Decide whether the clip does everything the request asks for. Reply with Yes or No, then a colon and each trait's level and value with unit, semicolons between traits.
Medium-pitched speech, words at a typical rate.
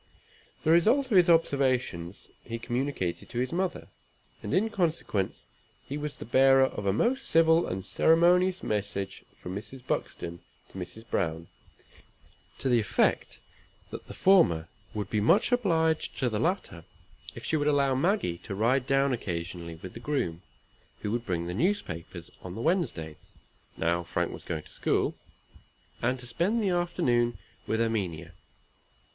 No: low, 125 Hz; average, 155 wpm